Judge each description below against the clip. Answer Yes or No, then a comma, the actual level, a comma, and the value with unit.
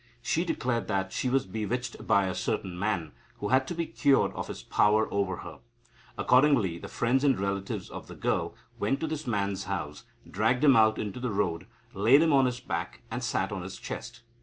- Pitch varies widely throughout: No, average, 4.8 semitones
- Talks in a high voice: No, low, 110 Hz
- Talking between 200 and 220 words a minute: Yes, fast, 205 wpm